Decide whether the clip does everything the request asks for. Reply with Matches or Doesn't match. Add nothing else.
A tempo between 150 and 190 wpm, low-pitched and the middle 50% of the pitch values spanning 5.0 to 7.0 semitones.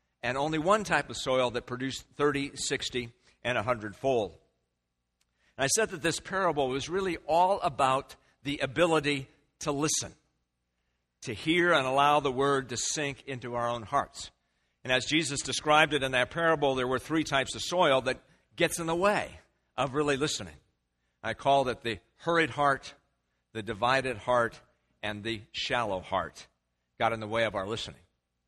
Matches